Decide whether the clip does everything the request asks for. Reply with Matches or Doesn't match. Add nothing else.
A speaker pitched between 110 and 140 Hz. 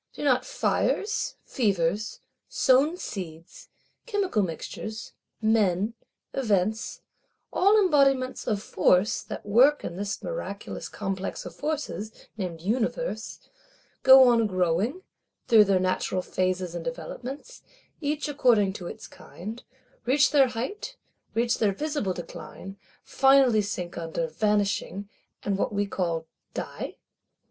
Doesn't match